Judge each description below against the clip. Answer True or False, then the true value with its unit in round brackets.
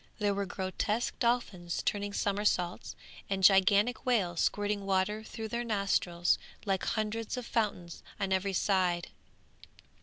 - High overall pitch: True (200 Hz)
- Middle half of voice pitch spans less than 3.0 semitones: True (2.4 semitones)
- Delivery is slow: True (125 wpm)